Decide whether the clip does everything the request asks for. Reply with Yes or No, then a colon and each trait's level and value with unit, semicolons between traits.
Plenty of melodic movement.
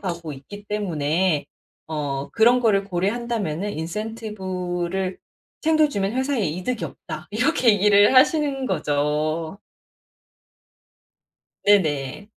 Yes: wide, 5.7 semitones